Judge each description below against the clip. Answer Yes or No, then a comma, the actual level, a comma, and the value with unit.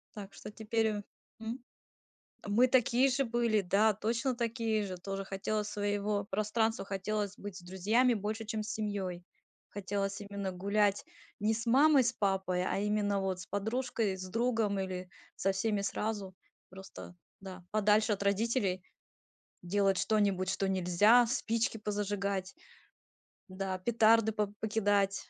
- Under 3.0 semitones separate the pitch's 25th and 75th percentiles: Yes, narrow, 2.4 semitones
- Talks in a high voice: Yes, high, 205 Hz